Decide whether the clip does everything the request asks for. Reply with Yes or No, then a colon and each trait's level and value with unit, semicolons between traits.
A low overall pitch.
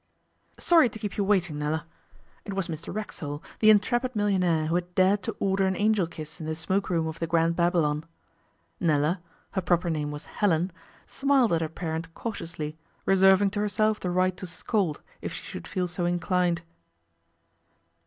No: medium, 180 Hz